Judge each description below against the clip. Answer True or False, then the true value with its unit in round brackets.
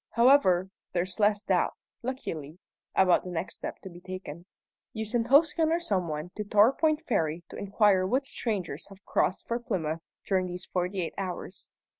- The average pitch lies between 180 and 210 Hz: True (190 Hz)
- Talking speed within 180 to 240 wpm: False (170 wpm)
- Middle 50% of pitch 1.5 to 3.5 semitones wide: False (4.7 semitones)